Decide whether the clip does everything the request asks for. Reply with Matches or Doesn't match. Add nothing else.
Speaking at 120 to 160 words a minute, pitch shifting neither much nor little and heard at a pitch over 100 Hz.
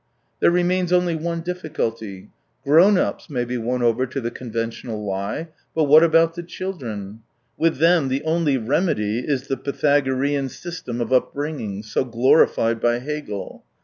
Doesn't match